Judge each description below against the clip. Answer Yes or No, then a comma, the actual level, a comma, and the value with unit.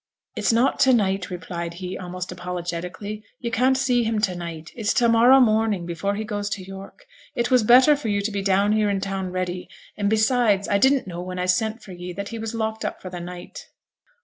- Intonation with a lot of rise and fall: No, average, 3.8 semitones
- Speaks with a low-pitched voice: No, high, 200 Hz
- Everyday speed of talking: No, fast, 225 wpm